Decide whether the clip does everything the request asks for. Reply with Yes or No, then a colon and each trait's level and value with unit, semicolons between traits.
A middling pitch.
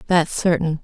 Yes: medium, 165 Hz